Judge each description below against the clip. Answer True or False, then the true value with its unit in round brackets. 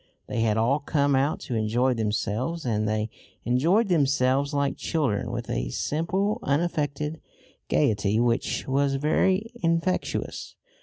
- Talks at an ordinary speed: False (125 wpm)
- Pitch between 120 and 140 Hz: True (135 Hz)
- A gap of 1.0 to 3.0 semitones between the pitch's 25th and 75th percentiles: False (5.4 semitones)